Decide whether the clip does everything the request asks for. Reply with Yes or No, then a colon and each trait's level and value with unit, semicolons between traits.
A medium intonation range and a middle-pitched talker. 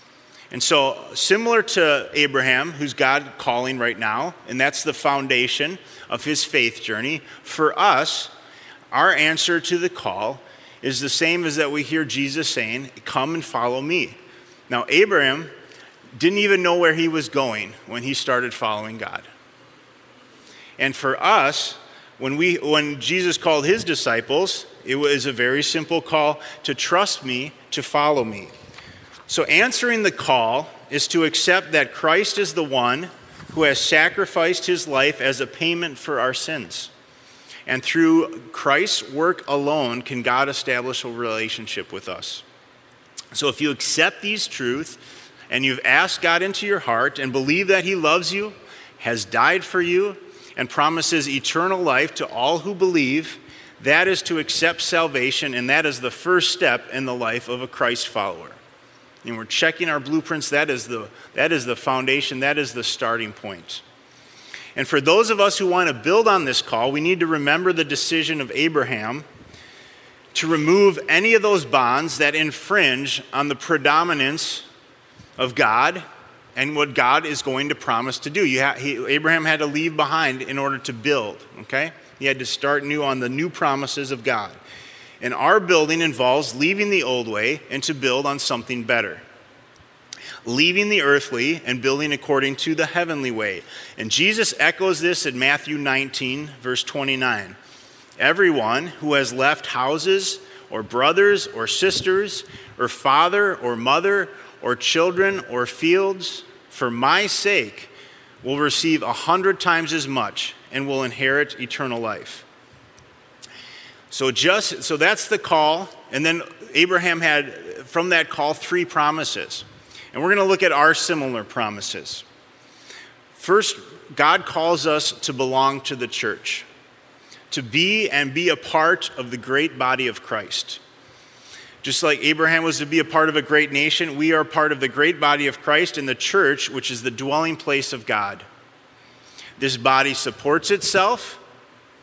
Yes: average, 4.2 semitones; medium, 150 Hz